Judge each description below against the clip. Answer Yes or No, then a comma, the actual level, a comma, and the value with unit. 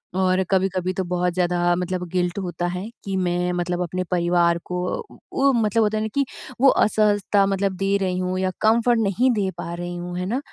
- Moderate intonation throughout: No, narrow, 2.3 semitones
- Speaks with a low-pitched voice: No, medium, 185 Hz